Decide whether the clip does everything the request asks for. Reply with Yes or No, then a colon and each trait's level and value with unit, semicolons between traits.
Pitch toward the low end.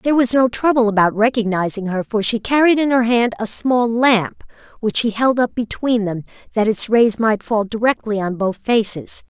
No: high, 225 Hz